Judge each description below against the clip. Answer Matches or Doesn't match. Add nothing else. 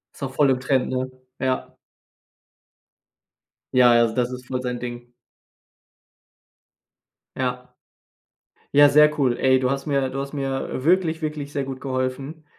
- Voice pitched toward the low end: Matches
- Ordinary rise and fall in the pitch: Doesn't match